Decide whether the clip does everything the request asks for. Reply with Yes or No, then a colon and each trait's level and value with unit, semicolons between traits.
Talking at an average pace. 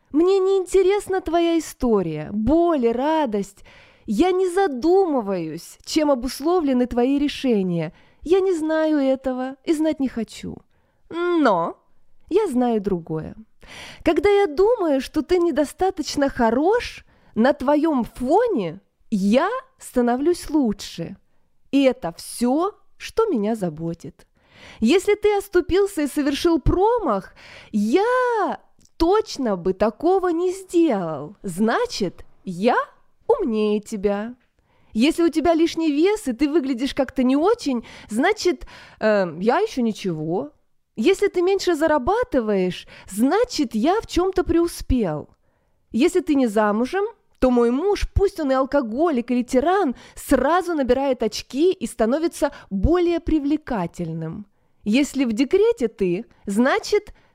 Yes: average, 115 wpm